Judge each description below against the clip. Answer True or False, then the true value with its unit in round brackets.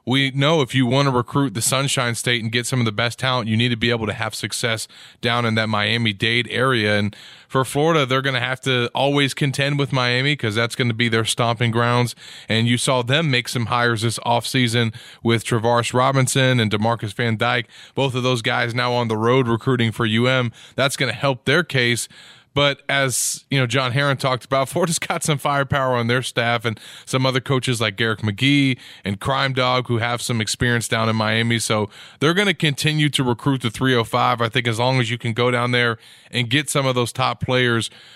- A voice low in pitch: True (125 Hz)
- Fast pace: True (225 wpm)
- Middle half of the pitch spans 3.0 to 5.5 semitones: False (2.4 semitones)